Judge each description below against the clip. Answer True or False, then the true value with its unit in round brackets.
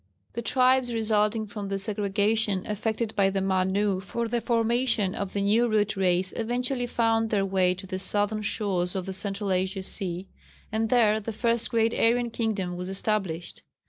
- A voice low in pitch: False (210 Hz)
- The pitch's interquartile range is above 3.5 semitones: False (2.8 semitones)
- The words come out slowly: False (175 wpm)